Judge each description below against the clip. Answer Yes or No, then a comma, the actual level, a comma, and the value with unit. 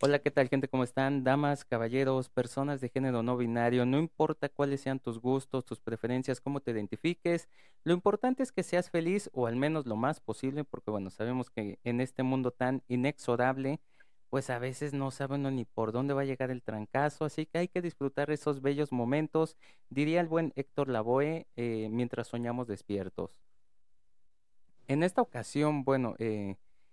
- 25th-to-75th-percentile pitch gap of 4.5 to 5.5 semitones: No, average, 3.4 semitones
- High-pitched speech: No, low, 135 Hz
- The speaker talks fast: No, average, 180 wpm